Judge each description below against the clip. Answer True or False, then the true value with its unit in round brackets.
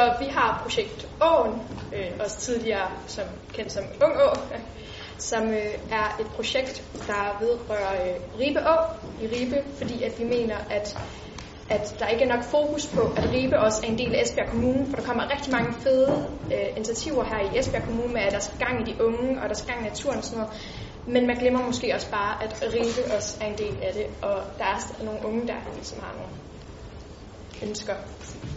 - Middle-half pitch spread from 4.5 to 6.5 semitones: False (3.4 semitones)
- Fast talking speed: False (210 wpm)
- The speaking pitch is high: True (235 Hz)